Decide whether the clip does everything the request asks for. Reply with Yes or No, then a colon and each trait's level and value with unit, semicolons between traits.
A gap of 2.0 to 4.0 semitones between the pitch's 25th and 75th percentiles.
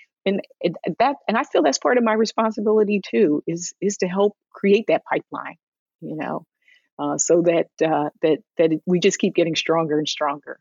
No: average, 4.6 semitones